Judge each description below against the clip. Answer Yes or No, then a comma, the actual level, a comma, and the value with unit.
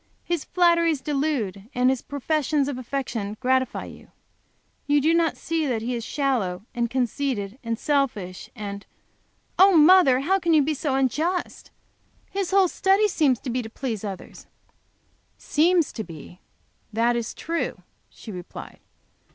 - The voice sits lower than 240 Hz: No, very high, 270 Hz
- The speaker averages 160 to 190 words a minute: No, average, 150 wpm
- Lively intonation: Yes, wide, 5.7 semitones